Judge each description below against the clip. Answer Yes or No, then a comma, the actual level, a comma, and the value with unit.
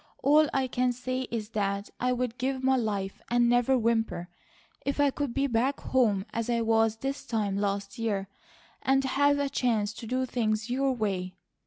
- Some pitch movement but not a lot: Yes, average, 3.4 semitones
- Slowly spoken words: No, average, 180 wpm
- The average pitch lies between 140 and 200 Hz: No, high, 240 Hz